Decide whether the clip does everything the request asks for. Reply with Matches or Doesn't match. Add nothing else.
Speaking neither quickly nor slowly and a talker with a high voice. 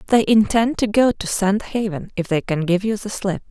Doesn't match